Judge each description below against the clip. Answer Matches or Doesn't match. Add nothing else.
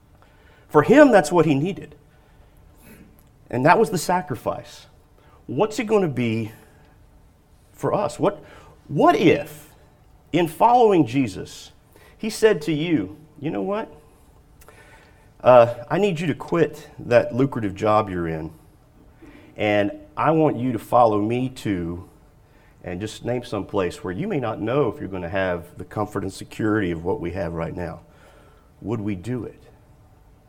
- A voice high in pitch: Doesn't match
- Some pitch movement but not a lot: Doesn't match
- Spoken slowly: Doesn't match